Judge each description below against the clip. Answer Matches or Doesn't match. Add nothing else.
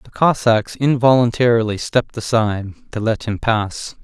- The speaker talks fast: Doesn't match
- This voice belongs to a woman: Doesn't match